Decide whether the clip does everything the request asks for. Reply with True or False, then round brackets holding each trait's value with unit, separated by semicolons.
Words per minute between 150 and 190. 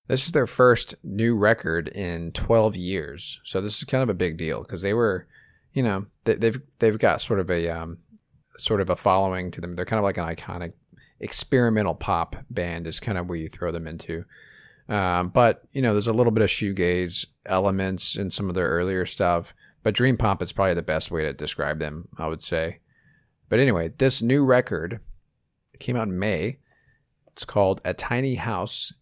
False (205 wpm)